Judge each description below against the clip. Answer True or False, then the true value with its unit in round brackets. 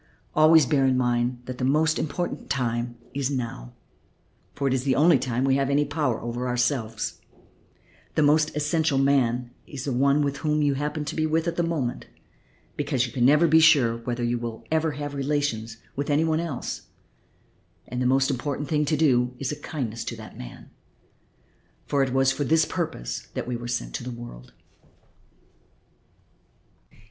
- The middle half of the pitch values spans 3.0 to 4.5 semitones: True (3.5 semitones)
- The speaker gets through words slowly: False (175 wpm)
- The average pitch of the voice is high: False (135 Hz)